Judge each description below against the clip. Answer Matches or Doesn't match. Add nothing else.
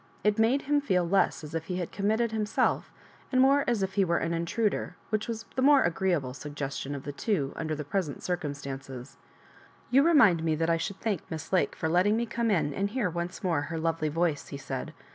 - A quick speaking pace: Matches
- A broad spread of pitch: Matches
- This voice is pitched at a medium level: Matches